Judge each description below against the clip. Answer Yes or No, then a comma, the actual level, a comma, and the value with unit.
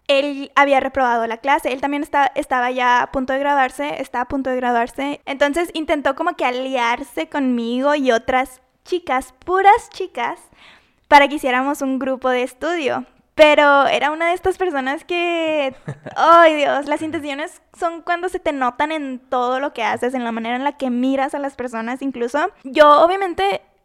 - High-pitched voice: Yes, very high, 280 Hz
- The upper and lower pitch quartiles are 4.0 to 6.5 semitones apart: No, average, 3.6 semitones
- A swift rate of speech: No, average, 180 wpm